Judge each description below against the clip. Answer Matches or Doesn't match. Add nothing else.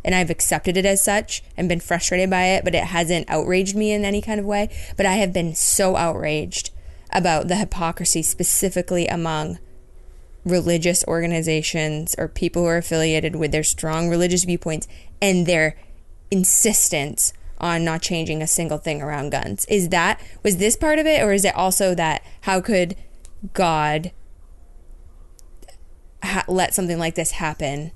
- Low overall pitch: Doesn't match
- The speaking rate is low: Doesn't match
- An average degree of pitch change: Matches